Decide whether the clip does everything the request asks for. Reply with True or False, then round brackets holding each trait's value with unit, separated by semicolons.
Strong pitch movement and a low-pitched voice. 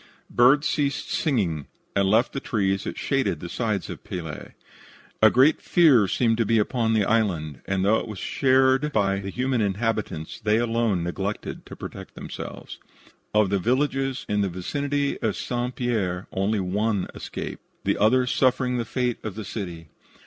False (4.5 semitones; 110 Hz)